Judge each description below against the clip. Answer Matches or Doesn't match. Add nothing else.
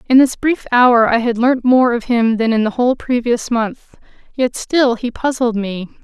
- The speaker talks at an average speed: Doesn't match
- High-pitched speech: Matches